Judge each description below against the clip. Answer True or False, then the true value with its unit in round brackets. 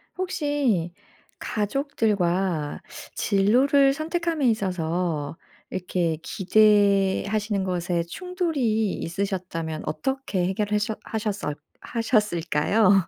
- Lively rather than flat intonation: False (4.9 semitones)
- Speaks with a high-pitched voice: True (205 Hz)